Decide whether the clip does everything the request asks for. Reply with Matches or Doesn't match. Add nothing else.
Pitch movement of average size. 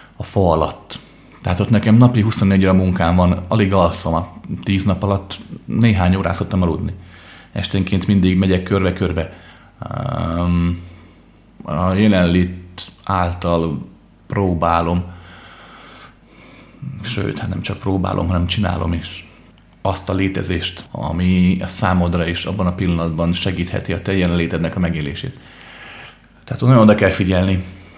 Doesn't match